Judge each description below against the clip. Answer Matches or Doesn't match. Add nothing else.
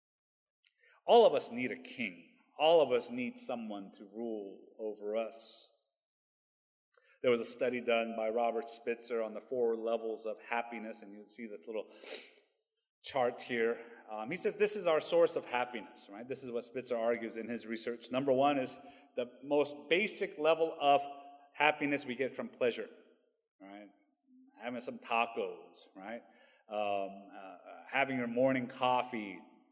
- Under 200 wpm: Matches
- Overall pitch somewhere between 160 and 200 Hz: Doesn't match